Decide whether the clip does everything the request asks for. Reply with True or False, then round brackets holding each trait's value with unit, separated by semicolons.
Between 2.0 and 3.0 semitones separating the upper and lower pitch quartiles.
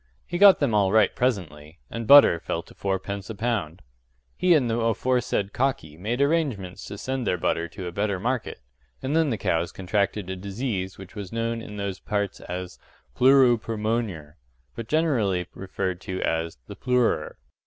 False (4.9 semitones)